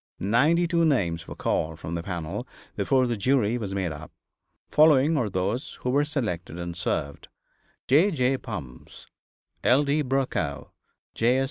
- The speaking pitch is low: Yes, low, 120 Hz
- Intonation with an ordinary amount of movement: No, wide, 8.3 semitones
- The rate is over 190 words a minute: No, average, 150 wpm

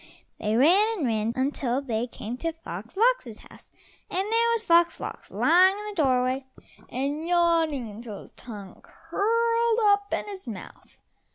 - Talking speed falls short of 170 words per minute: Yes, average, 160 wpm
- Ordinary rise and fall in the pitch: No, wide, 8.7 semitones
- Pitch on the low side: No, very high, 325 Hz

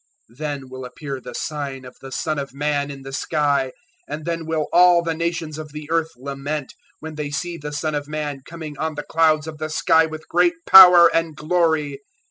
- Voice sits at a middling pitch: Yes, medium, 155 Hz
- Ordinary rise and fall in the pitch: No, narrow, 2.2 semitones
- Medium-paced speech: No, fast, 210 wpm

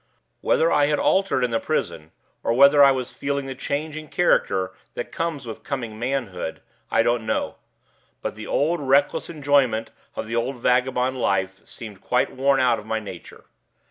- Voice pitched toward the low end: Yes, low, 130 Hz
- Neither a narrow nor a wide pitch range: Yes, average, 3.9 semitones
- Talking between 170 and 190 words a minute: Yes, average, 175 wpm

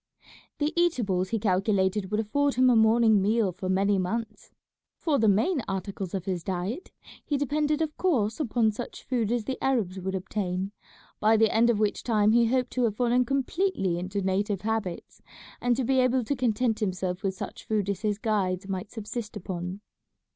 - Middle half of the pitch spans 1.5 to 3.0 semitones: No, average, 4.2 semitones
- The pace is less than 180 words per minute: No, average, 185 wpm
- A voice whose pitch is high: Yes, high, 215 Hz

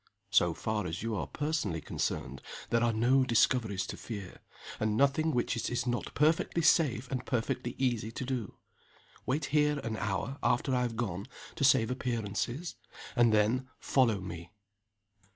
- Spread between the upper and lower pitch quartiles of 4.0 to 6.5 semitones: No, average, 3.6 semitones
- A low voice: Yes, low, 120 Hz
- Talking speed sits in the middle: Yes, average, 160 wpm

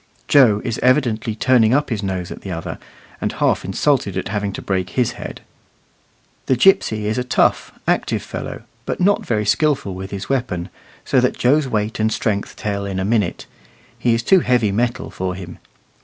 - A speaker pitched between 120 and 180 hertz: No, low, 110 Hz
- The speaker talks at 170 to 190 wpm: Yes, average, 185 wpm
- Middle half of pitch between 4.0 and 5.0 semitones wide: Yes, average, 4.3 semitones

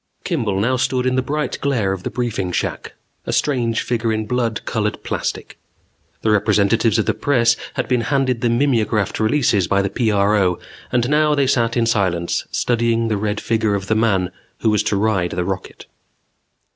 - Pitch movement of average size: Yes, average, 3.5 semitones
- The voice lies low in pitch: Yes, low, 115 Hz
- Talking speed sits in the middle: Yes, average, 185 wpm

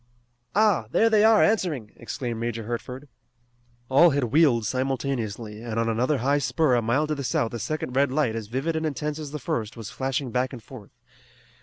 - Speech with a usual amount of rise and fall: Yes, average, 4.6 semitones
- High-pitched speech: No, low, 130 Hz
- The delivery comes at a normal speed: Yes, average, 195 wpm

